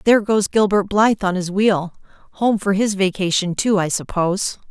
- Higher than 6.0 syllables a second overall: No, 5.2 syllables/s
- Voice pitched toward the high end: Yes, high, 195 Hz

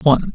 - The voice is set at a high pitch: No, medium, 145 Hz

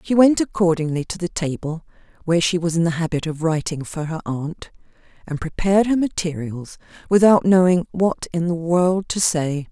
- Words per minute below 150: No, average, 180 wpm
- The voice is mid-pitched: Yes, medium, 170 Hz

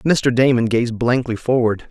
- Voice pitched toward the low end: Yes, low, 120 Hz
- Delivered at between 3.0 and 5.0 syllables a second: Yes, 4.3 syllables/s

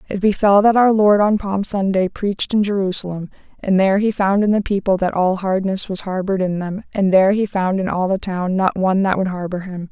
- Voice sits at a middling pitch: No, high, 195 Hz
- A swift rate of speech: Yes, fast, 235 wpm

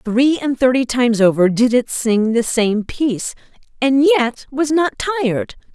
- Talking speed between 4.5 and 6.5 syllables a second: No, 4.3 syllables/s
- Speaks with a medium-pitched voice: No, very high, 250 Hz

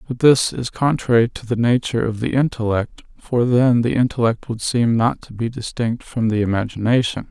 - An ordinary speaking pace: Yes, average, 190 wpm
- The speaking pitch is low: Yes, low, 120 Hz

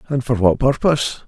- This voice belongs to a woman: No, male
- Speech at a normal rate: Yes, average, 190 wpm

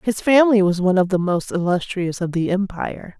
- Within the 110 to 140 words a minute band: No, fast, 205 wpm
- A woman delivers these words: Yes, female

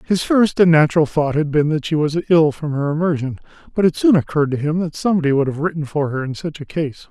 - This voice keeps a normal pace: No, fast, 260 wpm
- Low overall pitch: No, medium, 155 Hz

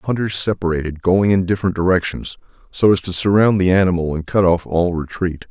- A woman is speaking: No, male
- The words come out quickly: No, average, 195 wpm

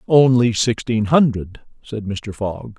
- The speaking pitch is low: Yes, low, 115 Hz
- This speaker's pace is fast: No, slow, 130 wpm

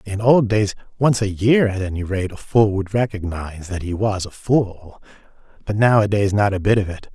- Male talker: Yes, male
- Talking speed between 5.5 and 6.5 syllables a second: No, 5.0 syllables/s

